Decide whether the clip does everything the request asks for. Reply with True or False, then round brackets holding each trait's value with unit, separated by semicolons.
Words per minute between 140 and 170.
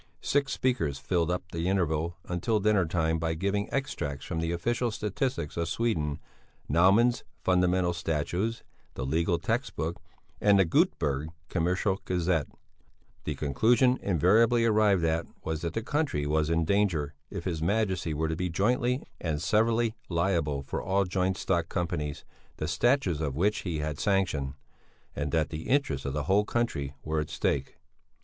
True (155 wpm)